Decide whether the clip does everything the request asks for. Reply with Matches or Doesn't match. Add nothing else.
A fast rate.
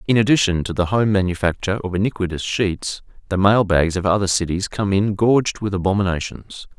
Doesn't match